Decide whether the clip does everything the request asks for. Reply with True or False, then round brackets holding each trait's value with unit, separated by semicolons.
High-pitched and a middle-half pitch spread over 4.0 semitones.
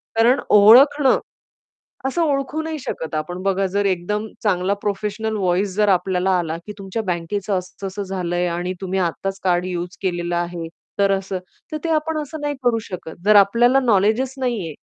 True (195 Hz; 4.4 semitones)